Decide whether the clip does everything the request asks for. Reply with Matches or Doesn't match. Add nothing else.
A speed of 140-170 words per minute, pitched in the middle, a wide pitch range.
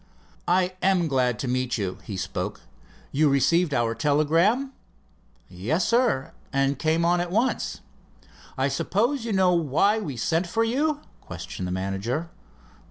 Matches